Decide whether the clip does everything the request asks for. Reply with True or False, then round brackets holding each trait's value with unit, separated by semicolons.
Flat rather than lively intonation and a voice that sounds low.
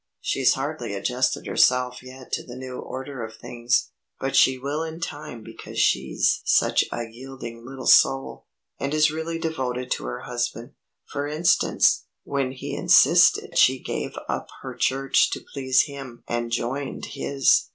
True (2.3 semitones; 130 Hz)